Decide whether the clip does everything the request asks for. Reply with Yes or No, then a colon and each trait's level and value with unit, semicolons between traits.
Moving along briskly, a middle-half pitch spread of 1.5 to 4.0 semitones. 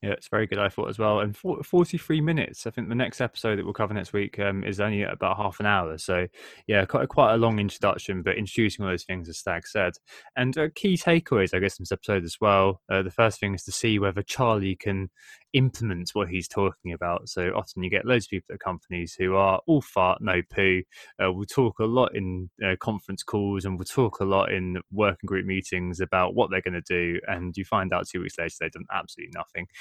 Yes: fast, 245 wpm; average, 3.0 semitones